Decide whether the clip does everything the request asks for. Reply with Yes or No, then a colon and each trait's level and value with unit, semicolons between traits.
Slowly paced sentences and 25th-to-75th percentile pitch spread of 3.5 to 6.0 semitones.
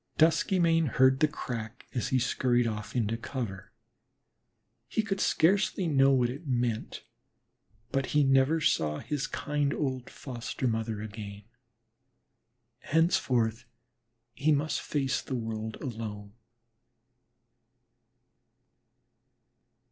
Yes: slow, 100 wpm; average, 4.7 semitones